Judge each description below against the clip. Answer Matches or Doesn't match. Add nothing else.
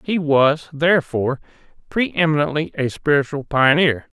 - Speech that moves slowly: Matches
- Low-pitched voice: Doesn't match